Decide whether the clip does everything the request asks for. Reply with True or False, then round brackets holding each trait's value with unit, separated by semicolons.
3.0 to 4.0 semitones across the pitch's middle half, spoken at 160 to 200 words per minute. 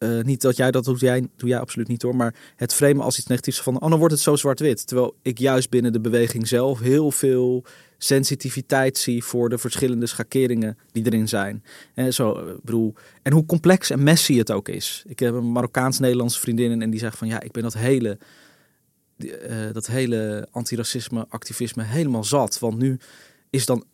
False (2.4 semitones; 195 wpm)